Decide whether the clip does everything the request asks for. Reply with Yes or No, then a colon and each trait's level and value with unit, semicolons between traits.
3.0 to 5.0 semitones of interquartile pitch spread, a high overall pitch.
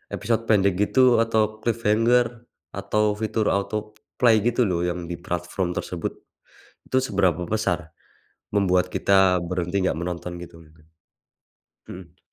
No: average, 3.7 semitones; low, 100 Hz